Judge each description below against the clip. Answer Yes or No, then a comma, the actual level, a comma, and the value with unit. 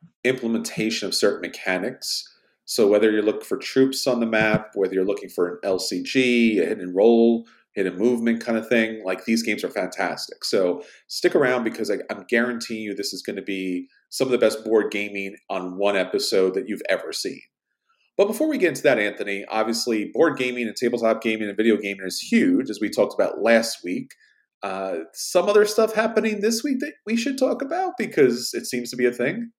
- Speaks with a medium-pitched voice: No, low, 115 Hz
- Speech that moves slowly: No, fast, 205 wpm